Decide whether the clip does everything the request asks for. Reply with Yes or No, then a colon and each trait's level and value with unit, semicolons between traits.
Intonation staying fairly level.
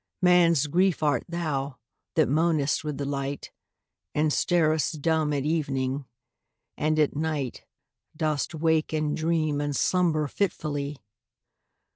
Yes: narrow, 2.1 semitones